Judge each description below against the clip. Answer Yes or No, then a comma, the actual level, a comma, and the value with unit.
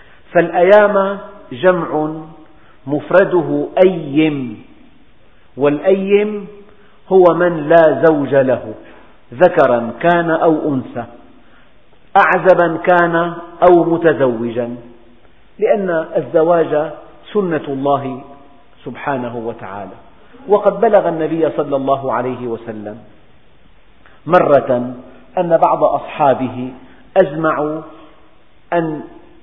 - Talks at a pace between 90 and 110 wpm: No, average, 75 wpm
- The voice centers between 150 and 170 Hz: Yes, medium, 155 Hz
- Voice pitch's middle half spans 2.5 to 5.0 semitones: No, wide, 5.4 semitones